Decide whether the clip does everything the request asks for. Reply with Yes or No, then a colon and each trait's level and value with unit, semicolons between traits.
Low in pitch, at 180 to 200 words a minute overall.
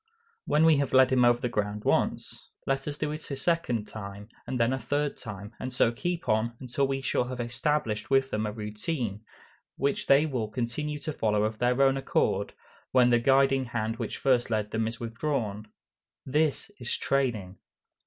Yes: low, 125 Hz; average, 190 wpm